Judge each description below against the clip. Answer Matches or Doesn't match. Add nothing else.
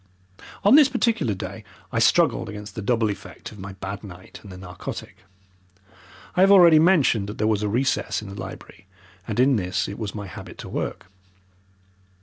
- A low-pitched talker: Matches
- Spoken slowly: Doesn't match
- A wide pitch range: Matches